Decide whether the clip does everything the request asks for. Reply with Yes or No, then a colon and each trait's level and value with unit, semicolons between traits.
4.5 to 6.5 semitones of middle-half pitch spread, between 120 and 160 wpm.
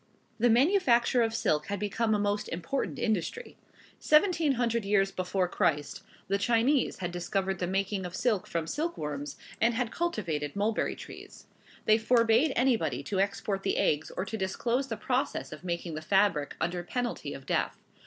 No: average, 4.9 semitones; average, 170 wpm